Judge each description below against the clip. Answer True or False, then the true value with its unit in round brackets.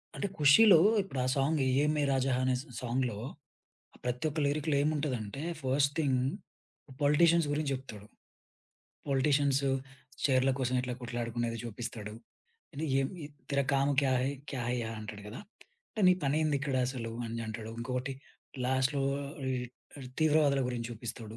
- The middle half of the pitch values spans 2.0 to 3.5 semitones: True (3.0 semitones)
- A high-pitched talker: False (135 Hz)